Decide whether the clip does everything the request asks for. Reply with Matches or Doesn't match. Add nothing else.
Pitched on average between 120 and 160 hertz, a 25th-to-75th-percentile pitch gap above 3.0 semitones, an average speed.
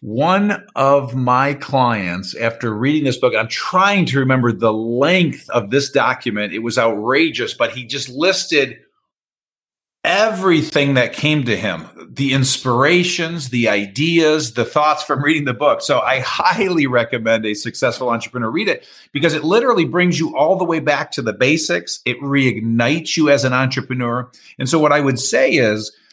Matches